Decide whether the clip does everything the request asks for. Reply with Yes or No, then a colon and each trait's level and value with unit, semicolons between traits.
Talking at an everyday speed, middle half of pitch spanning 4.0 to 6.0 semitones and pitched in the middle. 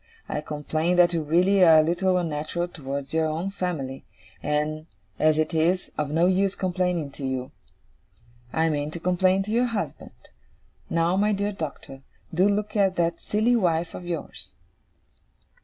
No: average, 160 wpm; average, 3.3 semitones; medium, 170 Hz